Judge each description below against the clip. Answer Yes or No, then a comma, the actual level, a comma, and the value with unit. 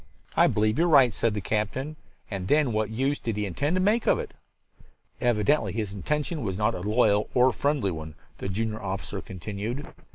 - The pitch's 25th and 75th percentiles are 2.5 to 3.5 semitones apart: No, average, 5.1 semitones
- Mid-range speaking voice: No, low, 110 Hz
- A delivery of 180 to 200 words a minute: Yes, average, 195 wpm